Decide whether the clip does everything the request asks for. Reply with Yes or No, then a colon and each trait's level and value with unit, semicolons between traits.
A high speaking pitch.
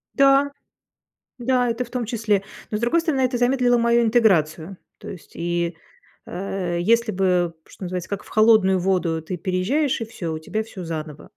Yes: high, 210 Hz